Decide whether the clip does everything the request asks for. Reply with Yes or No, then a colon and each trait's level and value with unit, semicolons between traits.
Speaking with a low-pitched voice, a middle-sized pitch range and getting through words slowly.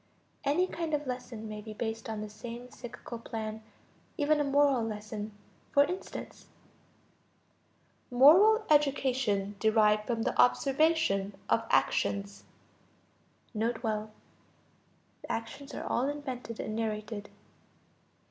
No: high, 230 Hz; average, 4.8 semitones; slow, 110 wpm